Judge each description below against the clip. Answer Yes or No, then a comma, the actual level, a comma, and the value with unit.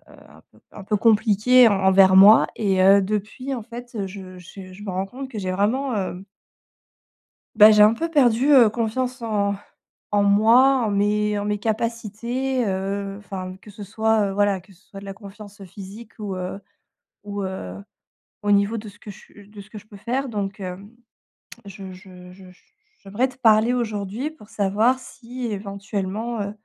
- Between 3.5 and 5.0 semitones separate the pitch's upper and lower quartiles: No, average, 2.8 semitones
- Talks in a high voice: Yes, high, 205 Hz